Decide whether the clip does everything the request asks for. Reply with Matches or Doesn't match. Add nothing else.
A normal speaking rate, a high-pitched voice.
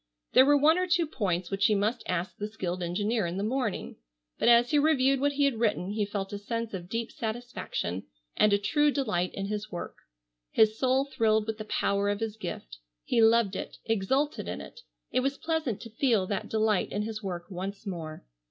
Doesn't match